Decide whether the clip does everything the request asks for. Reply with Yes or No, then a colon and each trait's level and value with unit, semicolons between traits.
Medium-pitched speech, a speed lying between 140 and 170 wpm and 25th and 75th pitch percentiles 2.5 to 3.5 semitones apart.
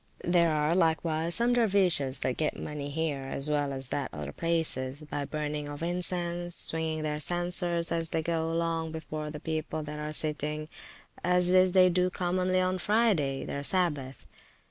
Yes: medium, 160 Hz; average, 165 wpm; average, 2.8 semitones